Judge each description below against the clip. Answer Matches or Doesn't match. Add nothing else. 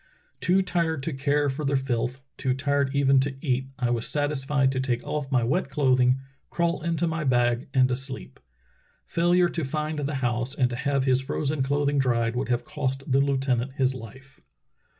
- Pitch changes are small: Matches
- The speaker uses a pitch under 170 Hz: Matches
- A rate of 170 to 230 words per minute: Matches